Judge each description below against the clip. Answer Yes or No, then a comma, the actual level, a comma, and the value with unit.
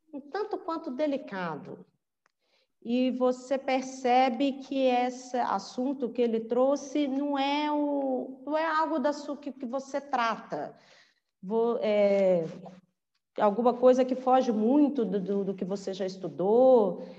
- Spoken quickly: No, average, 135 wpm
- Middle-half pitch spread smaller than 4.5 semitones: No, average, 4.8 semitones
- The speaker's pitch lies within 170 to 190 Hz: No, very high, 255 Hz